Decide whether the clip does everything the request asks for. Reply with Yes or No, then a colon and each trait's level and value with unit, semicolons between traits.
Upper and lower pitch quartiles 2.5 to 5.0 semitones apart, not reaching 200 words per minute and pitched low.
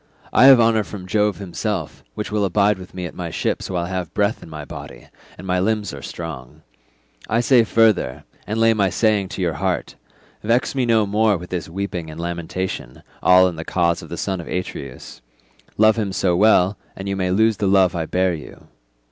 No: average, 3.6 semitones; fast, 205 wpm; very low, 95 Hz